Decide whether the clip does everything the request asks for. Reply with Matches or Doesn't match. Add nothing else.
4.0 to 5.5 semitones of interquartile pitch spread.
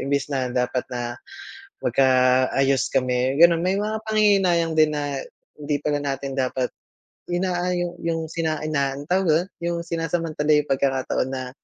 Matches